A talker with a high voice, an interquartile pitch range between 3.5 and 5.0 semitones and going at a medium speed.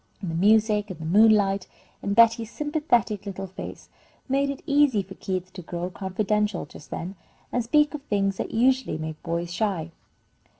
Yes: high, 205 Hz; average, 4.0 semitones; average, 170 wpm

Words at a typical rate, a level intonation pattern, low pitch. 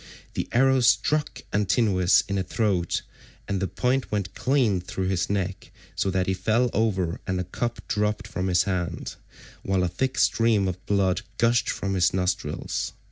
No: average, 170 wpm; average, 3.7 semitones; low, 100 Hz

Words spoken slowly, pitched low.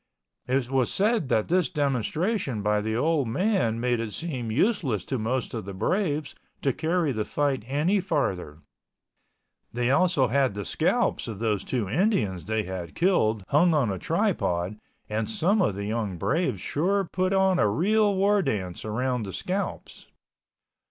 No: average, 165 wpm; low, 130 Hz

